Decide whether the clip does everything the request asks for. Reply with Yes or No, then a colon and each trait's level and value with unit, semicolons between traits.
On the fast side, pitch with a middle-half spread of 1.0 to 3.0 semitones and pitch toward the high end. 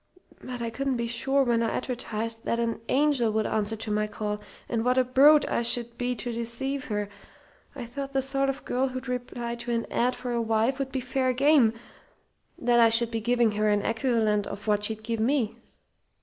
Yes: fast, 210 wpm; narrow, 2.4 semitones; high, 235 Hz